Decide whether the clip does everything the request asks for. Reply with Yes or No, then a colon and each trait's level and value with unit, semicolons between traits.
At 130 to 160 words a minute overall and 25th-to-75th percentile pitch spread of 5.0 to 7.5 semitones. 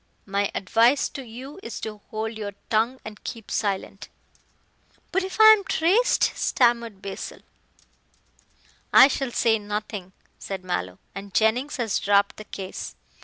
No: average, 140 wpm; average, 4.1 semitones